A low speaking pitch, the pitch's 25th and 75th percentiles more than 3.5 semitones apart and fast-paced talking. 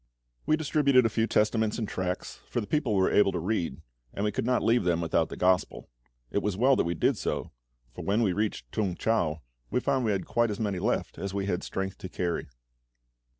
Yes: low, 105 Hz; average, 4.2 semitones; fast, 225 wpm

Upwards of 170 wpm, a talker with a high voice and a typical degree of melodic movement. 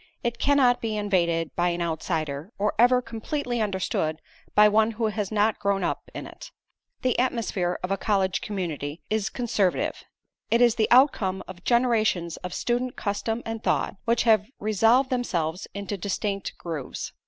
No: average, 160 wpm; high, 210 Hz; average, 4.4 semitones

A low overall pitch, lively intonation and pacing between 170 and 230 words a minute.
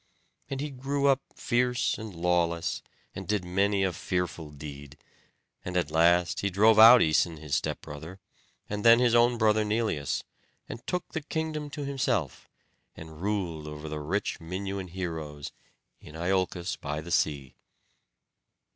No: very low, 90 Hz; wide, 6.3 semitones; average, 145 wpm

